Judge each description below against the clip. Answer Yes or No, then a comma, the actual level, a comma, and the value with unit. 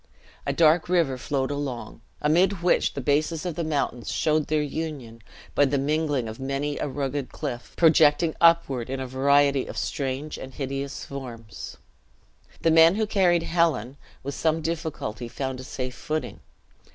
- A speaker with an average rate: Yes, average, 160 wpm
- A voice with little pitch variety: No, average, 3.4 semitones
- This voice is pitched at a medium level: Yes, medium, 145 Hz